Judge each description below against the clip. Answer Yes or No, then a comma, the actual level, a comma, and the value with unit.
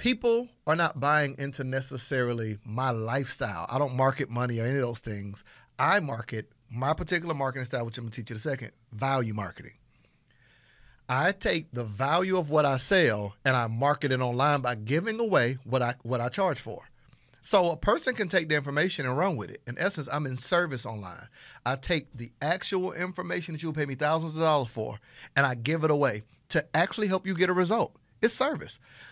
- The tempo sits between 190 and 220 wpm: Yes, fast, 205 wpm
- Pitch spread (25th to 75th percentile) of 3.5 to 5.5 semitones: Yes, average, 5.1 semitones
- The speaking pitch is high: No, low, 135 Hz